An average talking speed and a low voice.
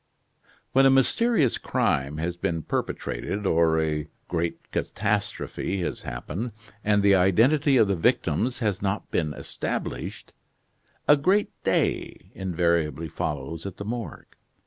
No: slow, 125 wpm; very low, 95 Hz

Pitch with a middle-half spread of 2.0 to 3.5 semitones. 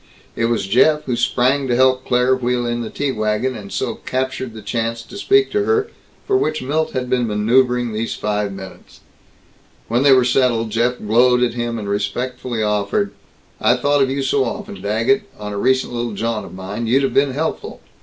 Yes: average, 3.1 semitones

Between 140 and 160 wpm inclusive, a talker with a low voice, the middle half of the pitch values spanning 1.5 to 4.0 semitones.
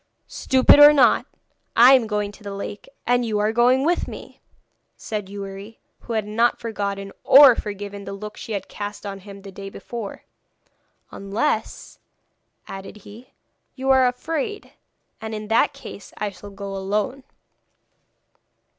No: average, 150 wpm; high, 210 Hz; average, 3.6 semitones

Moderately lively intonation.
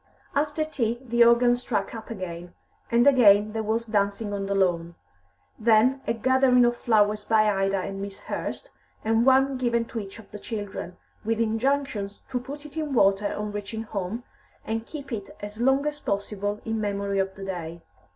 Yes: average, 3.4 semitones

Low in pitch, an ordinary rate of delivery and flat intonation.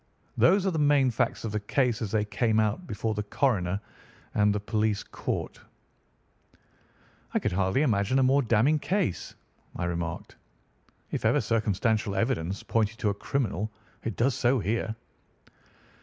No: low, 110 Hz; average, 155 wpm; average, 4.1 semitones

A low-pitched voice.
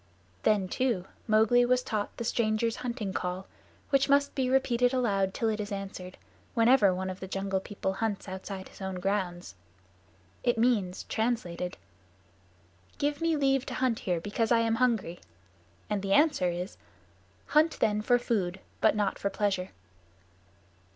No: high, 210 Hz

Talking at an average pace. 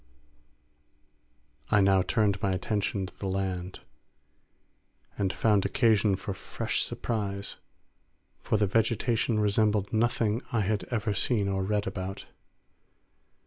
No: slow, 115 wpm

